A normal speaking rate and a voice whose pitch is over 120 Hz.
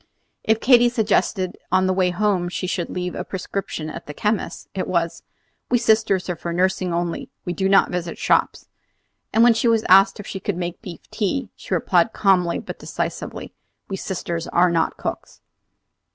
Yes: average, 185 wpm; medium, 185 Hz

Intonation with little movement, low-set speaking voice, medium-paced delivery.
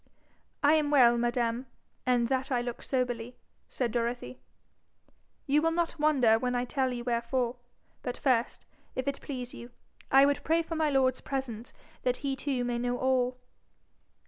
No: narrow, 2.3 semitones; very high, 250 Hz; average, 165 wpm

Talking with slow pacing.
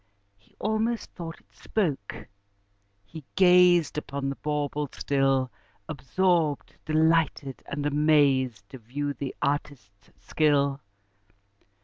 Yes: slow, 100 wpm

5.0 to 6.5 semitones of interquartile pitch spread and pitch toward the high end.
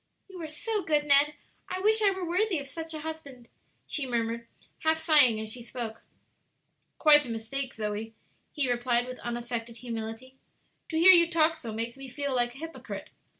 Yes: average, 5.3 semitones; very high, 270 Hz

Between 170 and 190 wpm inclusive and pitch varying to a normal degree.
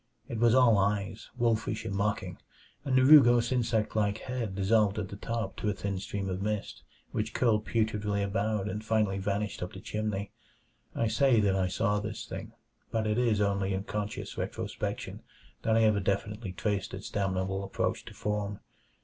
No: average, 180 wpm; narrow, 2.2 semitones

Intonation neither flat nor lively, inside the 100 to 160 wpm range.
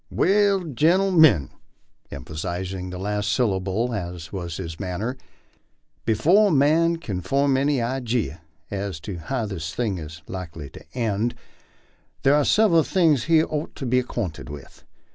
No: wide, 8.2 semitones; average, 150 wpm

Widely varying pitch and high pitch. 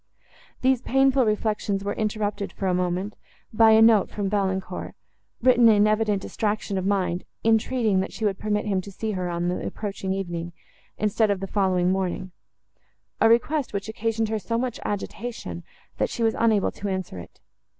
No: average, 2.8 semitones; high, 205 Hz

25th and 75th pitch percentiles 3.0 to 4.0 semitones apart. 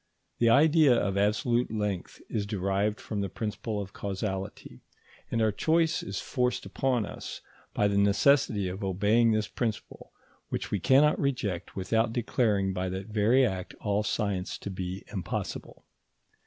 Yes: average, 3.3 semitones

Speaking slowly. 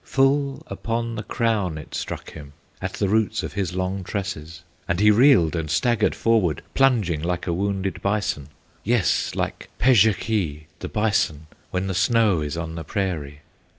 No: average, 160 wpm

